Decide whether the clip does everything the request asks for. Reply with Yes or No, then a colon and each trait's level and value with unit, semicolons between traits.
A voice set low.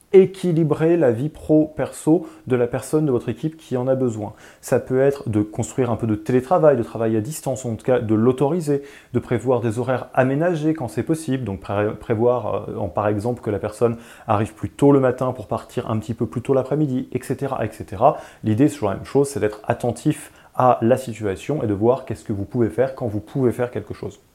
Yes: low, 125 Hz